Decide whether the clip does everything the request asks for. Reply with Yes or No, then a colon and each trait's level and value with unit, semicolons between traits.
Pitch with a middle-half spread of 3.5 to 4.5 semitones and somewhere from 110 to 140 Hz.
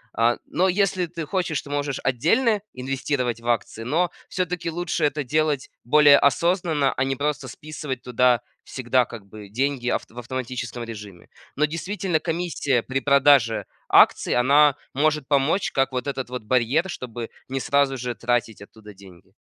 Yes: average, 4.1 semitones; low, 135 Hz